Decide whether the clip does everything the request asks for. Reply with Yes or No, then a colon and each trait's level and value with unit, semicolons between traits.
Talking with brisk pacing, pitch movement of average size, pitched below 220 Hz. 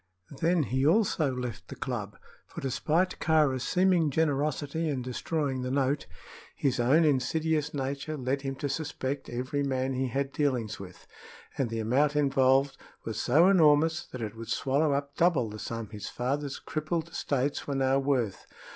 No: average, 165 wpm; average, 3.0 semitones; medium, 140 Hz